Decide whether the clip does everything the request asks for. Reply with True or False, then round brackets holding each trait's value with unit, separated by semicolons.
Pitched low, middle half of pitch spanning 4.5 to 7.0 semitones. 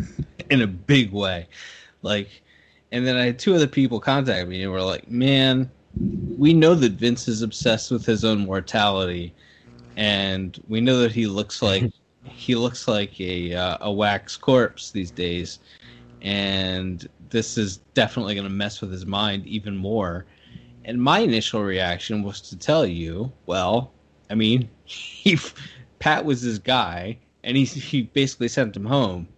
True (105 Hz; 4.9 semitones)